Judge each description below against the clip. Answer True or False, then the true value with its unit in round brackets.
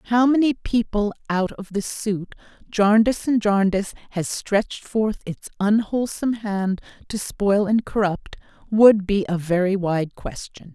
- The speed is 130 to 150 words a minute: True (145 wpm)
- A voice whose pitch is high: True (205 Hz)